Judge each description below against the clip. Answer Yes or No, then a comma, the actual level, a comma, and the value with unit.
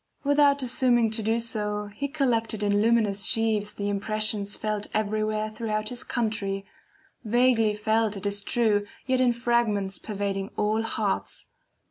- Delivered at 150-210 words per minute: No, average, 140 wpm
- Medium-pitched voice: No, high, 215 Hz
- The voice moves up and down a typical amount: No, narrow, 2.2 semitones